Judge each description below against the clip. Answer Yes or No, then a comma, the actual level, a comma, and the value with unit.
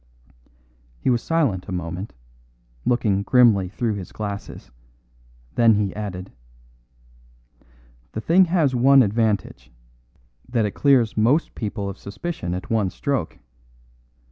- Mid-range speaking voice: No, low, 110 Hz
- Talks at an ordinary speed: No, slow, 115 wpm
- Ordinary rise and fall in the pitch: Yes, average, 4.2 semitones